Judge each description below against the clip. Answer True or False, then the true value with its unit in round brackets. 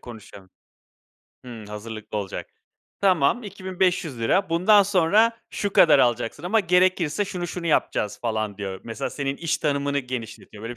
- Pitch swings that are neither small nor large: False (8.4 semitones)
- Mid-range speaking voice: True (145 Hz)